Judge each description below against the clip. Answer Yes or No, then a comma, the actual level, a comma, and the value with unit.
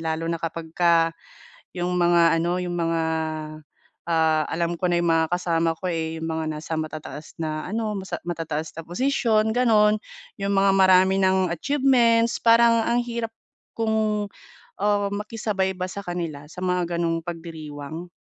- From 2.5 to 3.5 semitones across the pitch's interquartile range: No, average, 4.2 semitones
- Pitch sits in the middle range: Yes, medium, 175 Hz